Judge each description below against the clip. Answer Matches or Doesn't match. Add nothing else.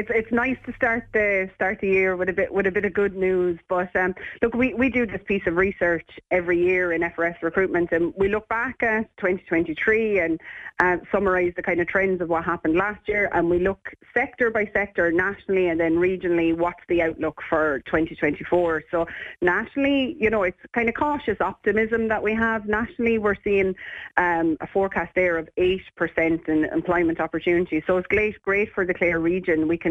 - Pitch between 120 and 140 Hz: Doesn't match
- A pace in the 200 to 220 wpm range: Matches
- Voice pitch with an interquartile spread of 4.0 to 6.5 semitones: Doesn't match